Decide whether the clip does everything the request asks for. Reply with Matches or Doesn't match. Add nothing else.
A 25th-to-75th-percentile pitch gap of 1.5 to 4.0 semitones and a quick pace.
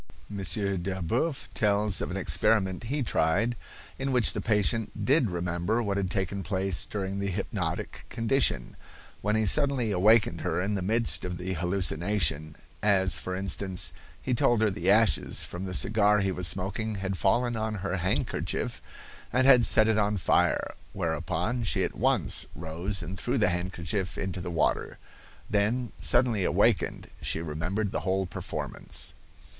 Doesn't match